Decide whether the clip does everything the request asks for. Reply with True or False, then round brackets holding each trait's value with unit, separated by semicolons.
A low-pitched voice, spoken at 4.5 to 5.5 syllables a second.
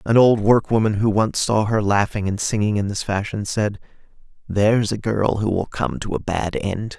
True (105 Hz; 4.8 syllables/s)